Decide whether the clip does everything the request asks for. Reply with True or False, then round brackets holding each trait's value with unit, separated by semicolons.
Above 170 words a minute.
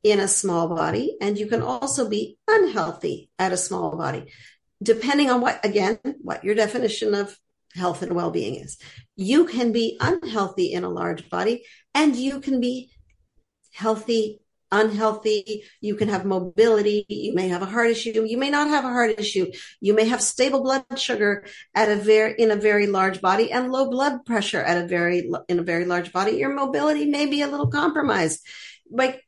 True (185 wpm)